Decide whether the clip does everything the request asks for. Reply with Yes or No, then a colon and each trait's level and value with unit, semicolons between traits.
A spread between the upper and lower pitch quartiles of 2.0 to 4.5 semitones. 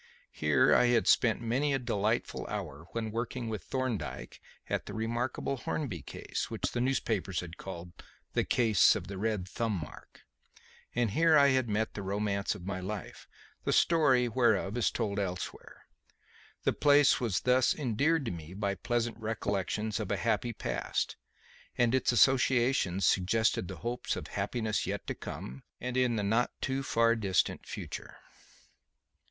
Yes: average, 3.9 semitones